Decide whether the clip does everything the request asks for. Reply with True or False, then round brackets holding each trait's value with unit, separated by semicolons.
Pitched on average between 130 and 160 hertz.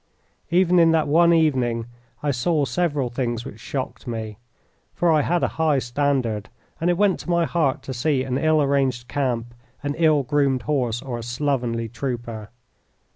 True (135 Hz)